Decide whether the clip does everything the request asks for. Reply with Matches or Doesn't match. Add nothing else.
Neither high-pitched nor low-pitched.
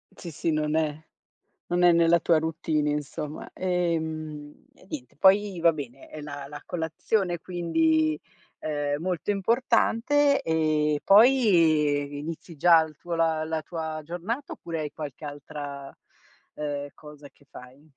Matches